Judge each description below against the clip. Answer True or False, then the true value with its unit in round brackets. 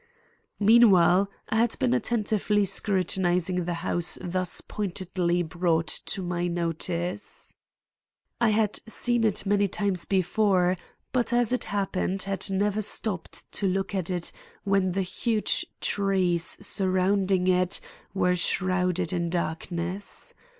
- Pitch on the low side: False (185 Hz)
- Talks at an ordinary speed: False (120 wpm)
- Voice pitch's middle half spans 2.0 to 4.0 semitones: True (2.4 semitones)